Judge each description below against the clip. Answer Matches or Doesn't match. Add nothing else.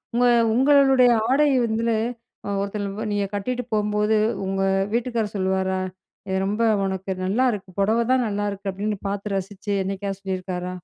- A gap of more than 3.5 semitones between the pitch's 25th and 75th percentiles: Doesn't match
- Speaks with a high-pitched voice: Matches